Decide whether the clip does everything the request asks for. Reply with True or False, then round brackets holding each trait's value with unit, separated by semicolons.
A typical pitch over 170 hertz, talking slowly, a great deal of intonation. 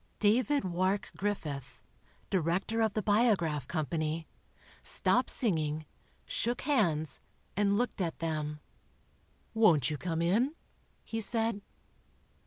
True (185 Hz; 105 wpm; 6.0 semitones)